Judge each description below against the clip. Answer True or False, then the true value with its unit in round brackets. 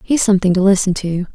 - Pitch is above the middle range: True (195 Hz)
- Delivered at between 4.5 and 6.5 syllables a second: False (6.7 syllables/s)